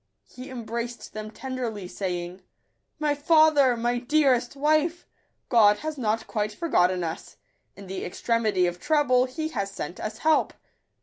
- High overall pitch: Yes, high, 240 Hz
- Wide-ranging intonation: Yes, wide, 5.9 semitones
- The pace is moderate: Yes, average, 150 wpm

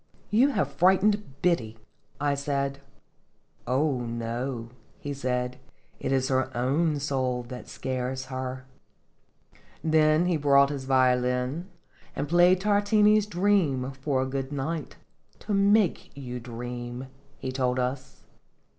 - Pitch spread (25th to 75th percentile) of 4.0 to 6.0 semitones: Yes, average, 4.5 semitones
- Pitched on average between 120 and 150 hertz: Yes, low, 135 Hz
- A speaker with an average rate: No, slow, 130 wpm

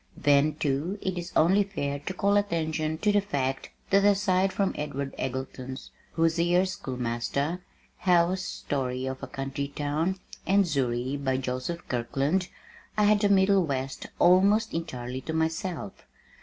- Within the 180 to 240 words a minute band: No, average, 140 wpm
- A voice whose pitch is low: No, medium, 160 Hz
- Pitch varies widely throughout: Yes, wide, 5.7 semitones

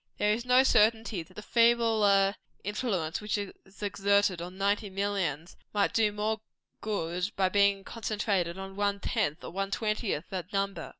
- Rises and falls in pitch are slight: Yes, narrow, 1.9 semitones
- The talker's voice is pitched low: No, high, 200 Hz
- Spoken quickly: No, average, 165 wpm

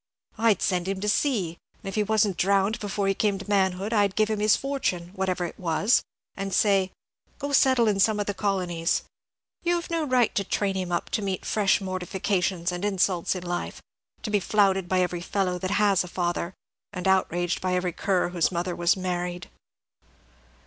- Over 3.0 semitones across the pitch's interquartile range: No, narrow, 2.6 semitones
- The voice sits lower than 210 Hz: Yes, high, 190 Hz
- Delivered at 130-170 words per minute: No, average, 195 wpm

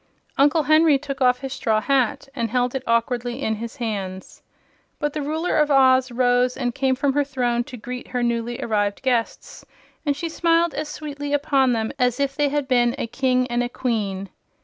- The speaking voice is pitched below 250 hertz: No, very high, 255 Hz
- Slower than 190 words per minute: No, average, 195 wpm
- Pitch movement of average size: Yes, average, 3.1 semitones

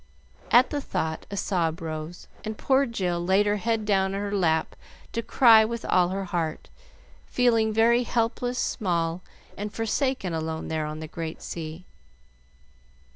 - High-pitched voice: Yes, high, 195 Hz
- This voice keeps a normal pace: Yes, average, 155 wpm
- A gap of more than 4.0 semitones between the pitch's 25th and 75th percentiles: Yes, wide, 5.5 semitones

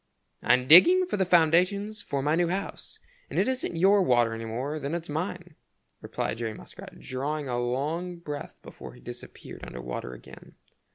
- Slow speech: No, average, 175 wpm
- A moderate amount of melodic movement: No, wide, 6.4 semitones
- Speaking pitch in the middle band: Yes, medium, 155 Hz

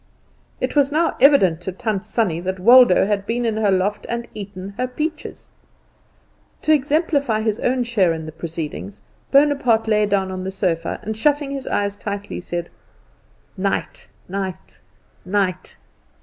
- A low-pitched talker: No, high, 205 Hz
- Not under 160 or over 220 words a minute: No, average, 150 wpm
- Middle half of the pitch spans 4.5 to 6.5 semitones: Yes, average, 5.1 semitones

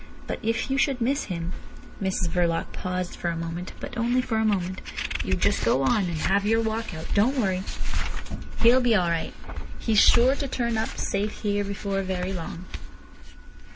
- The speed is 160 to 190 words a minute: Yes, average, 185 wpm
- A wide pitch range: No, average, 4.3 semitones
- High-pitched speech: Yes, high, 200 Hz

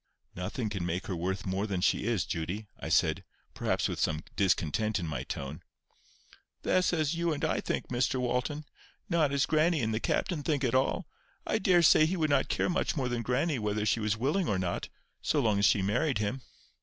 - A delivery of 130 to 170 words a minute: No, fast, 205 wpm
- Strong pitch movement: Yes, wide, 7.4 semitones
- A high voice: No, low, 120 Hz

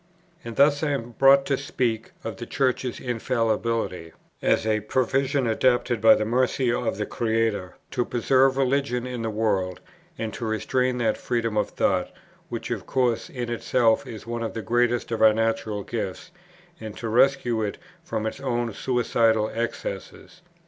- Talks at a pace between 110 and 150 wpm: No, average, 165 wpm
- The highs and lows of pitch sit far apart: No, narrow, 2.4 semitones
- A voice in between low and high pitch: No, low, 115 Hz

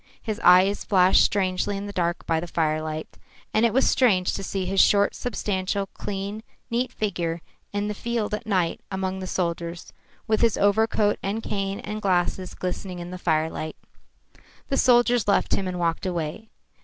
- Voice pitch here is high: Yes, high, 195 Hz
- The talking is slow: No, average, 170 wpm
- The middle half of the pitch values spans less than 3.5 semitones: Yes, average, 2.9 semitones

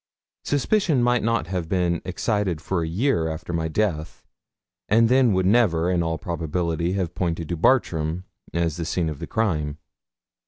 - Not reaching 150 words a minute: No, average, 165 wpm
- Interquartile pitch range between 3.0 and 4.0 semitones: No, average, 4.6 semitones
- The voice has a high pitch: No, very low, 90 Hz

